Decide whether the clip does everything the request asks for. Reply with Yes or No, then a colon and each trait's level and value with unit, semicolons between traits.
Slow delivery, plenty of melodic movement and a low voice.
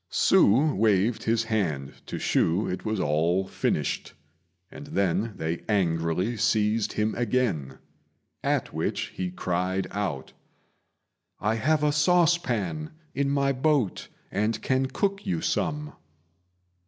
Yes: slow, 120 wpm; wide, 6.8 semitones; low, 110 Hz